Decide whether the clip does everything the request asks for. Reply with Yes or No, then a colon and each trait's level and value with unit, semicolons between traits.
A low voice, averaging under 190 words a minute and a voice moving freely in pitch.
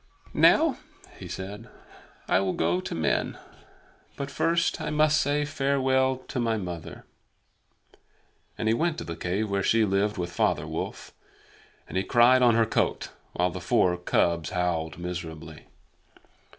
Yes: low, 100 Hz; average, 150 wpm; wide, 6.8 semitones